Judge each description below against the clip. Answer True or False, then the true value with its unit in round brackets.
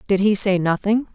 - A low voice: False (200 Hz)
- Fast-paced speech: True (210 wpm)